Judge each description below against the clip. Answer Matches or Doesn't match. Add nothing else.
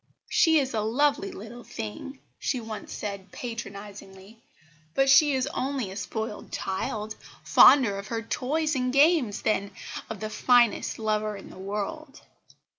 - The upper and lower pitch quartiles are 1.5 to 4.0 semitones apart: Doesn't match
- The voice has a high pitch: Matches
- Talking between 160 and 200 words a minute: Doesn't match